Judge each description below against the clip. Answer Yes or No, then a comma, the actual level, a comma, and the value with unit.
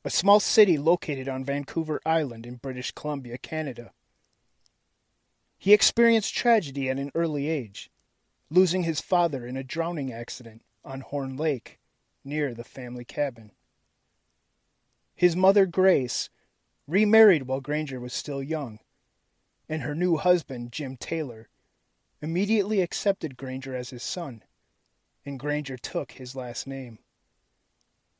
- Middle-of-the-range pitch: Yes, medium, 145 Hz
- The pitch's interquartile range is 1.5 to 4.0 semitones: No, average, 4.9 semitones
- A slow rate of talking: Yes, slow, 125 wpm